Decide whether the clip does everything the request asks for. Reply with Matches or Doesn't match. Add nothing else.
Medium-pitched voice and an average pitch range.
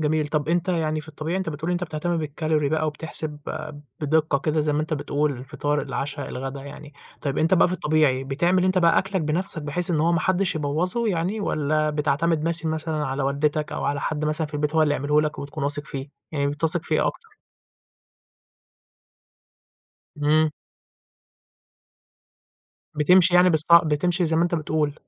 Doesn't match